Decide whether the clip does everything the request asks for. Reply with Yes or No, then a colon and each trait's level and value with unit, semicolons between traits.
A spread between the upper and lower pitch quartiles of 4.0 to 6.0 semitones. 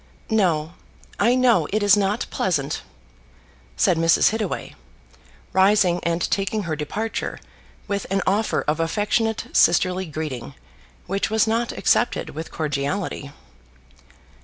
Yes: average, 4.8 semitones